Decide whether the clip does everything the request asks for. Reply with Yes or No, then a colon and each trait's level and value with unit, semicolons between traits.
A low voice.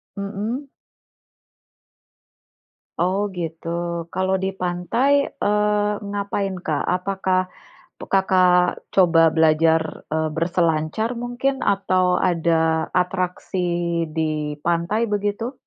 No: medium, 185 Hz